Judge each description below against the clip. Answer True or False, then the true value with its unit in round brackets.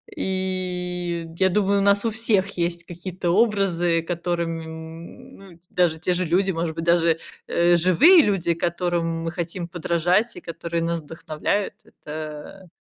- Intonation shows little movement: True (2.1 semitones)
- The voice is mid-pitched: True (175 Hz)